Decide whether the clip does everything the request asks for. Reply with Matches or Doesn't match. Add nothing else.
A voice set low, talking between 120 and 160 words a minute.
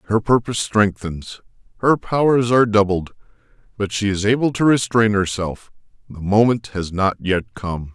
Matches